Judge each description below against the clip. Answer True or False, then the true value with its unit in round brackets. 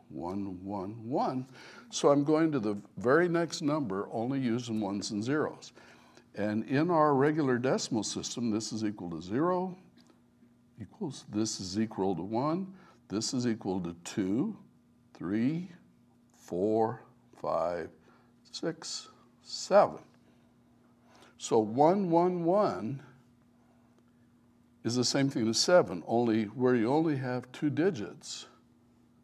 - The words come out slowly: True (125 wpm)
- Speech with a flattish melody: False (5.0 semitones)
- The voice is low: True (120 Hz)